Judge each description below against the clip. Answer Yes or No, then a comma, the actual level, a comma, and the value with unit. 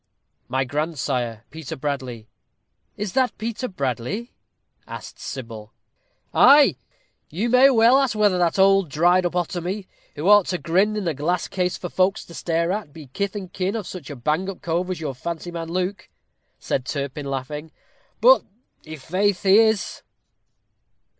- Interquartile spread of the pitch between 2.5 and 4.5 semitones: No, average, 5.1 semitones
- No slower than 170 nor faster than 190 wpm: No, average, 160 wpm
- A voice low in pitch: No, medium, 175 Hz